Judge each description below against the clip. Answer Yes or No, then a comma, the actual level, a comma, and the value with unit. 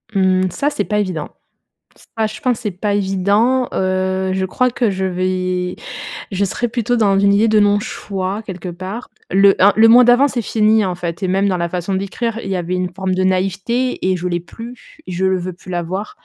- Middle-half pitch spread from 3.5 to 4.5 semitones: No, average, 2.8 semitones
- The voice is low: No, high, 195 Hz